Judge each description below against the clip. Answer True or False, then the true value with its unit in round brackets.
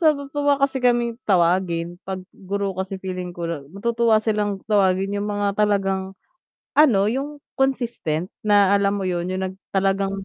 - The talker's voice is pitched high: True (200 Hz)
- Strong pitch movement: False (3.4 semitones)